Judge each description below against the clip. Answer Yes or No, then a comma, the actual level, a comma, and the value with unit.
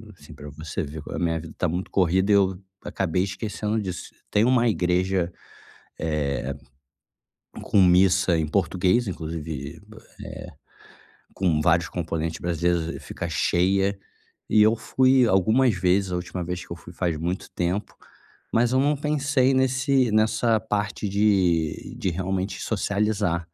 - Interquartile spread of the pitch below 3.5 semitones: No, average, 3.9 semitones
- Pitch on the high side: No, very low, 95 Hz